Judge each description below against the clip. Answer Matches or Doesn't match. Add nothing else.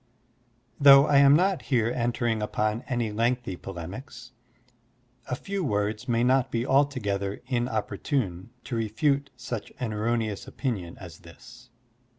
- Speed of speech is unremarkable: Doesn't match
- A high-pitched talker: Doesn't match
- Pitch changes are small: Doesn't match